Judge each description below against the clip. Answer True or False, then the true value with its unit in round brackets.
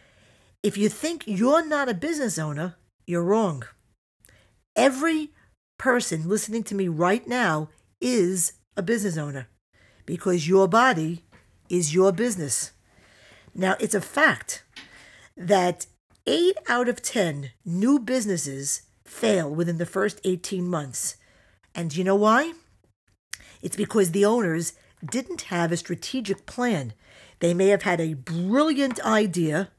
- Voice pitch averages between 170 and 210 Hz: True (185 Hz)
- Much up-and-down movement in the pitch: True (5.9 semitones)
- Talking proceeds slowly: True (130 wpm)